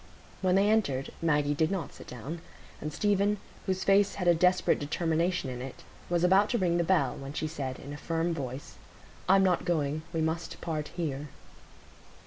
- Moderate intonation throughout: Yes, average, 4.0 semitones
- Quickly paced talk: No, average, 185 wpm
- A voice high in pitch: No, medium, 165 Hz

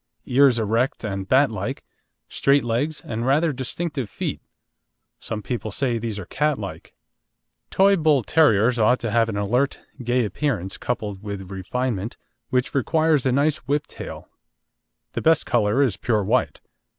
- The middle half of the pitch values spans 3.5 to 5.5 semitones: Yes, average, 4.7 semitones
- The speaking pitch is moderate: No, low, 125 Hz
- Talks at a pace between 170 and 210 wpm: No, average, 150 wpm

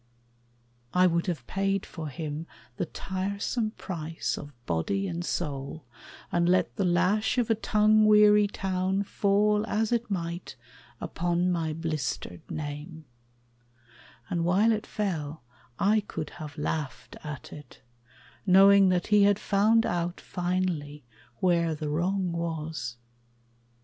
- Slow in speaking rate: Yes, slow, 130 wpm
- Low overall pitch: No, medium, 175 Hz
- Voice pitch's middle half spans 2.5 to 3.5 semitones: No, average, 4.1 semitones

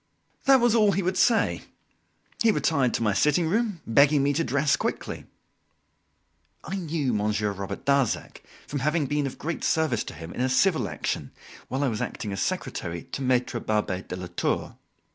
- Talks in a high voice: No, medium, 140 Hz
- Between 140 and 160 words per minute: No, average, 175 wpm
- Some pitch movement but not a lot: No, wide, 7.5 semitones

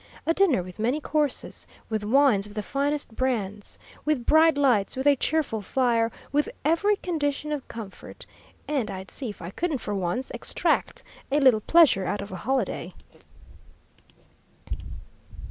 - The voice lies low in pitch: No, very high, 260 Hz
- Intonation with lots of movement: Yes, wide, 6.1 semitones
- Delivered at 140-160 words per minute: Yes, average, 150 wpm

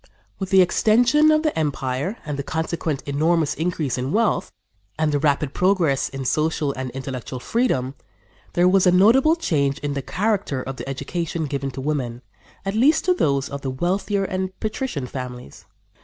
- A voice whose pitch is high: No, medium, 155 Hz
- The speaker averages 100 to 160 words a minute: No, average, 175 wpm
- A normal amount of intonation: No, wide, 6.1 semitones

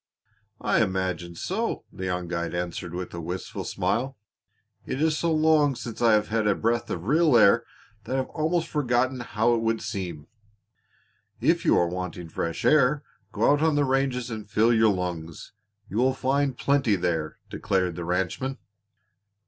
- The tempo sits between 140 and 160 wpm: No, average, 170 wpm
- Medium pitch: No, low, 115 Hz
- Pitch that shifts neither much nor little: No, wide, 6.9 semitones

